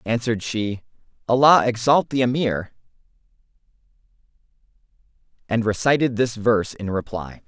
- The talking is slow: Yes, slow, 95 wpm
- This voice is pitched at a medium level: No, low, 115 Hz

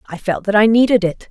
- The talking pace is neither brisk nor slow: No, fast, 275 wpm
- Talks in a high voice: Yes, high, 205 Hz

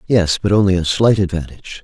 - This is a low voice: Yes, very low, 95 Hz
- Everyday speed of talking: Yes, average, 195 wpm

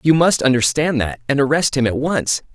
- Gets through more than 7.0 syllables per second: No, 5.3 syllables/s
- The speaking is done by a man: Yes, male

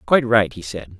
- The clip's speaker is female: No, male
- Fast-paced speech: Yes, fast, 240 wpm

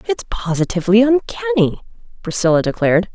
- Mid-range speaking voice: No, high, 215 Hz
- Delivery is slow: Yes, slow, 95 wpm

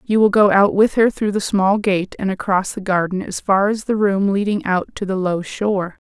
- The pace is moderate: No, fast, 245 wpm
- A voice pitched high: Yes, high, 195 Hz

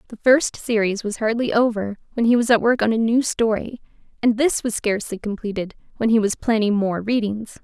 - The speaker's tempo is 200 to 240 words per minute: Yes, fast, 205 wpm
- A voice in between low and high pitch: No, high, 220 Hz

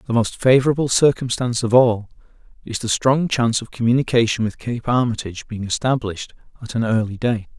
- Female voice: No, male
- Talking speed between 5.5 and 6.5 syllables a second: Yes, 6.1 syllables/s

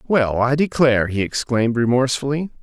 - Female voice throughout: No, male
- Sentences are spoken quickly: No, slow, 135 wpm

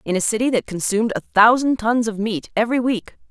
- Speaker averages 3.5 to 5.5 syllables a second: No, 5.9 syllables/s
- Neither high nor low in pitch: No, high, 220 Hz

